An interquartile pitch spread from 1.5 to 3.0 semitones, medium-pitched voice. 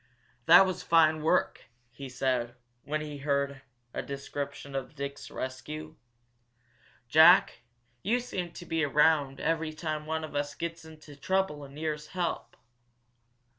Yes: narrow, 2.5 semitones; medium, 150 Hz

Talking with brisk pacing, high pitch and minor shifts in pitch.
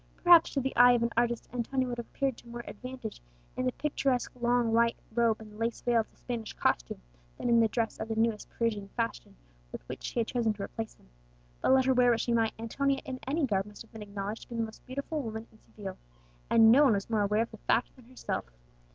Yes: fast, 245 wpm; high, 235 Hz; narrow, 2.3 semitones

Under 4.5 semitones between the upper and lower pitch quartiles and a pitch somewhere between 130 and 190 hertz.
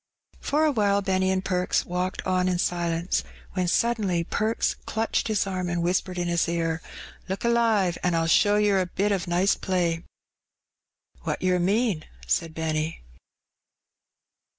Yes: average, 2.7 semitones; medium, 185 Hz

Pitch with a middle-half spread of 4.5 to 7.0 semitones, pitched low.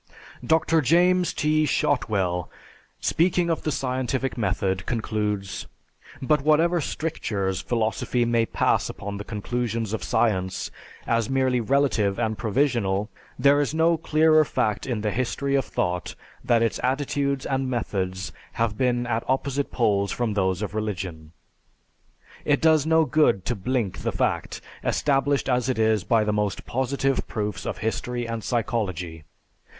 Yes: average, 5.0 semitones; low, 120 Hz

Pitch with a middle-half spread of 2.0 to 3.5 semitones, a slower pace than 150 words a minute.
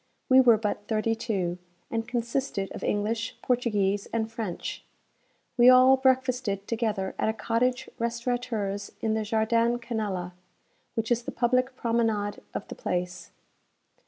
Yes: average, 2.8 semitones; slow, 135 wpm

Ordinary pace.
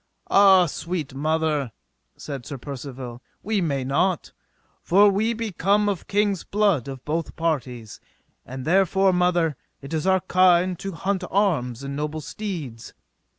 Yes: average, 145 wpm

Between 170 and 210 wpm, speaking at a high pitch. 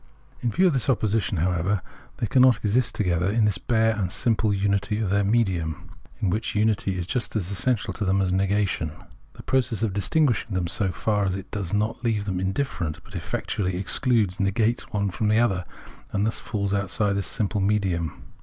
No: average, 190 wpm; low, 100 Hz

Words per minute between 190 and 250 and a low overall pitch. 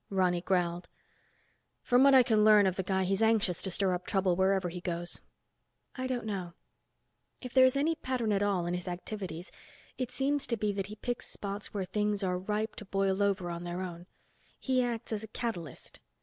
No: average, 200 wpm; high, 200 Hz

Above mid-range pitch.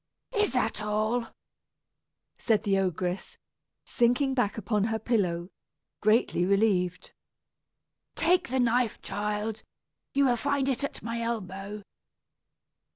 Yes: high, 220 Hz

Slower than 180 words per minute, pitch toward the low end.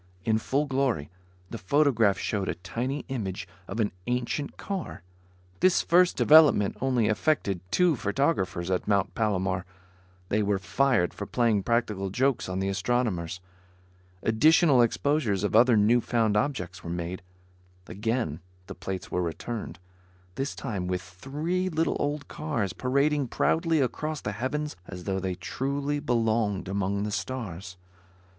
Yes: average, 140 wpm; low, 115 Hz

